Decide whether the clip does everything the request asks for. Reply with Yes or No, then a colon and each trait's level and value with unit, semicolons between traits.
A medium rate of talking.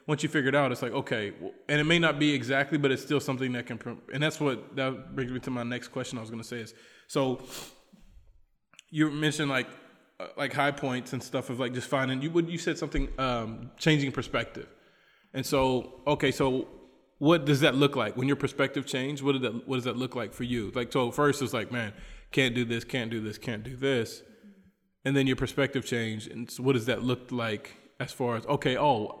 No: fast, 230 wpm